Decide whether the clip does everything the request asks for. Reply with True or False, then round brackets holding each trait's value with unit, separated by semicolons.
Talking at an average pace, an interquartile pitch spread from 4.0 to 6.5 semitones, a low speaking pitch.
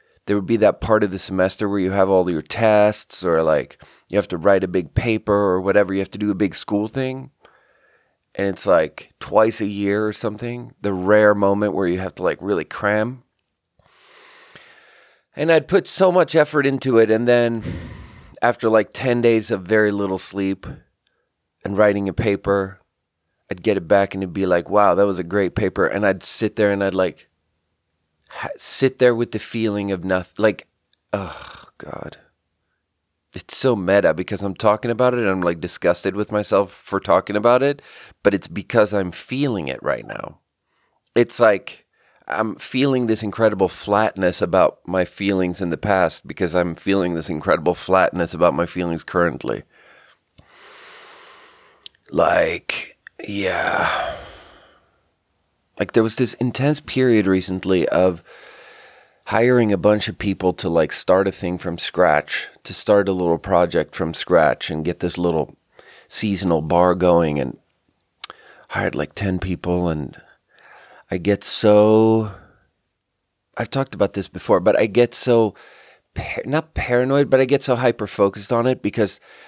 False (165 wpm; 3.6 semitones; 100 Hz)